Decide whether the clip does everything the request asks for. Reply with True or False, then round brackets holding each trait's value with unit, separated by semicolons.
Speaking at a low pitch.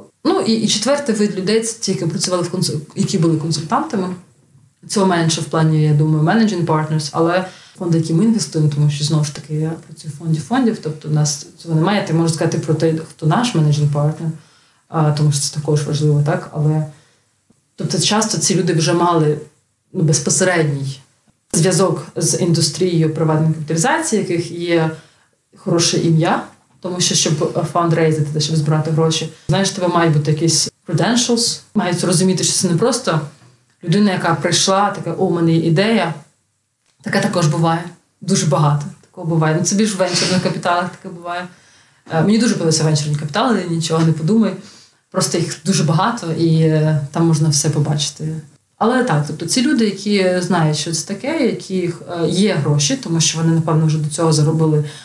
False (165 Hz)